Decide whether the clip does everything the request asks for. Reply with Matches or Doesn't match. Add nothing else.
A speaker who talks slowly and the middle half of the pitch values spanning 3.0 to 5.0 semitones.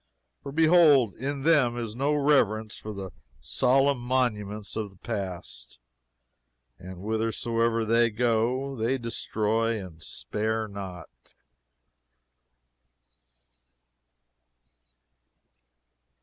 Matches